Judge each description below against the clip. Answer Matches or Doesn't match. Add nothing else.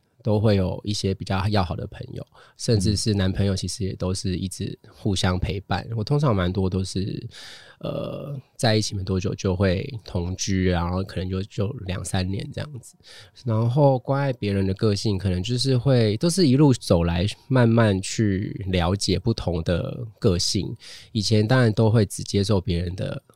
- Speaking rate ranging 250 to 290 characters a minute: Matches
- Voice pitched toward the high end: Doesn't match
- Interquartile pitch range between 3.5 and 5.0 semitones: Matches